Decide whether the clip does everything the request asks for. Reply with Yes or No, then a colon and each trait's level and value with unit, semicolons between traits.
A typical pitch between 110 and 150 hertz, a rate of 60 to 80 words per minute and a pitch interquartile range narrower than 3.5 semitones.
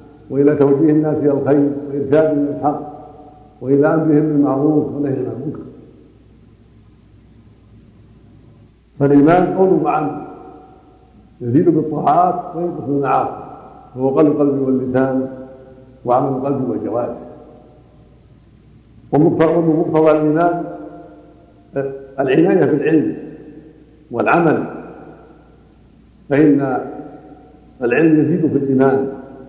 Yes: medium, 140 Hz; average, 75 wpm; narrow, 2.5 semitones